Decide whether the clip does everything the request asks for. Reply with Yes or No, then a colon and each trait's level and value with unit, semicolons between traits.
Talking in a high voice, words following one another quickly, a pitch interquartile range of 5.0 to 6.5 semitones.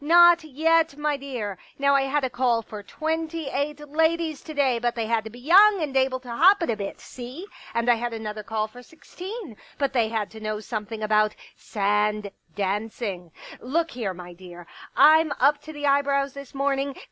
Yes: very high, 260 Hz; fast, 210 wpm; wide, 5.6 semitones